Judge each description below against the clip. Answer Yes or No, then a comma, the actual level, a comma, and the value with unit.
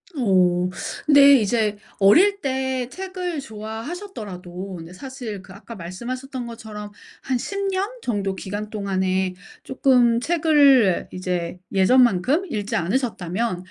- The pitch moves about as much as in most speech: No, wide, 5.9 semitones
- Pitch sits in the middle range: No, high, 225 Hz